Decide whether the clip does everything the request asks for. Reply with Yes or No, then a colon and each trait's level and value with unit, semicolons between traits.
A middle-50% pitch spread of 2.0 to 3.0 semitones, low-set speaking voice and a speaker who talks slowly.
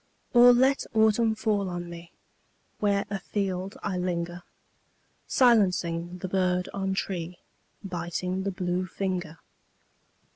No: narrow, 2.4 semitones; medium, 185 Hz; slow, 110 wpm